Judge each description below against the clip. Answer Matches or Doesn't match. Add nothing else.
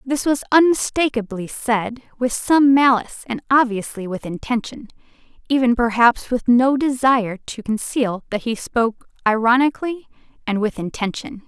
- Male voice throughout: Doesn't match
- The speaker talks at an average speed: Doesn't match